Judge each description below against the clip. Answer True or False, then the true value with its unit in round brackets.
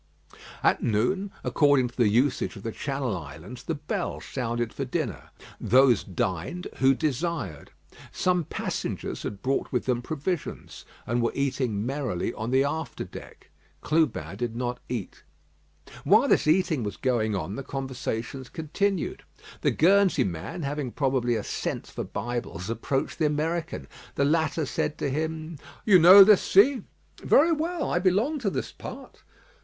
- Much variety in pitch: True (5.7 semitones)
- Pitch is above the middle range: False (135 Hz)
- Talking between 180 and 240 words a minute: False (150 wpm)